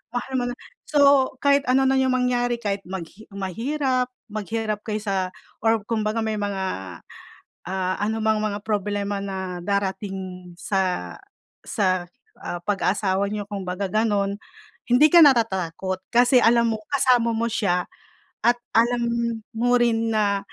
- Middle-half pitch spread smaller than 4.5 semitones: Yes, average, 3.6 semitones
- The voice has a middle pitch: No, high, 215 Hz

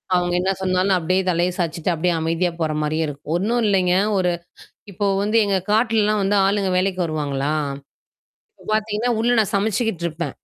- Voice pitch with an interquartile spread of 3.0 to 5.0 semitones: Yes, average, 3.7 semitones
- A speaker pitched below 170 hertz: No, medium, 185 Hz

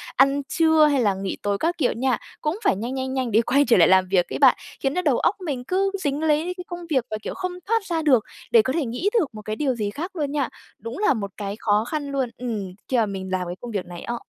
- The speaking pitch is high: Yes, very high, 260 Hz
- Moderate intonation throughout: No, wide, 6.2 semitones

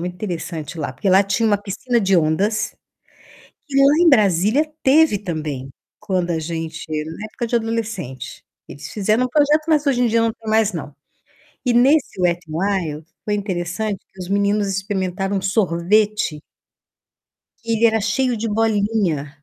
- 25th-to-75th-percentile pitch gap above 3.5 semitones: Yes, average, 4.6 semitones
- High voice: Yes, high, 200 Hz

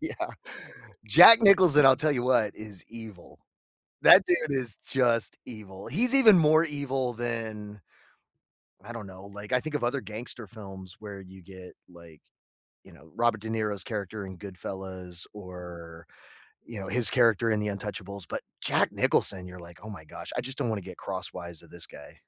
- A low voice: Yes, low, 105 Hz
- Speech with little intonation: No, average, 4.6 semitones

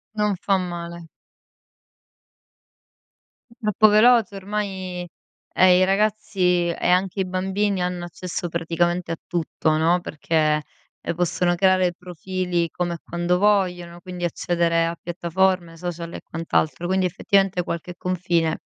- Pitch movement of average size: No, narrow, 1.8 semitones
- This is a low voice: No, medium, 180 Hz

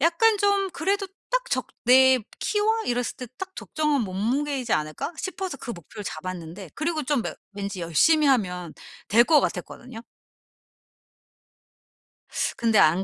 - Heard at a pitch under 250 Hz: No, very high, 255 Hz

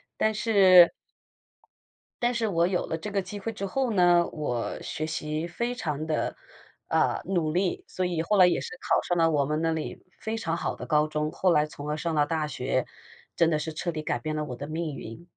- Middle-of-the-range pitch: Yes, medium, 165 Hz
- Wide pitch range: No, average, 3.3 semitones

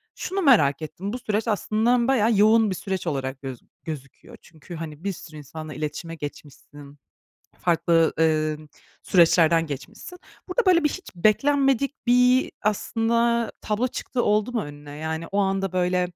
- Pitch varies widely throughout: Yes, wide, 6.9 semitones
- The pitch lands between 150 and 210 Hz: Yes, high, 190 Hz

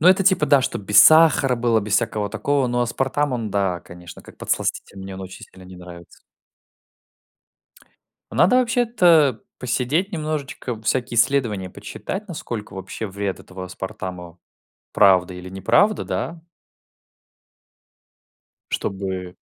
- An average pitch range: No, wide, 7.7 semitones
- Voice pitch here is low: Yes, low, 115 Hz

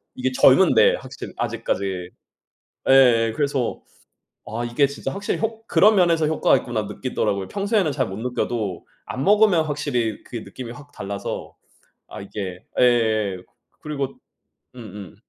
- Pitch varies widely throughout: Yes, wide, 6.1 semitones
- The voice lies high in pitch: No, low, 125 Hz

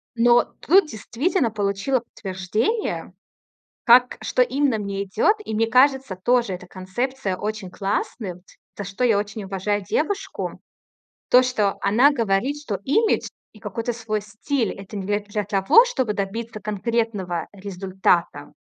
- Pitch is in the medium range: No, high, 215 Hz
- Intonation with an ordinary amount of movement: Yes, average, 4.2 semitones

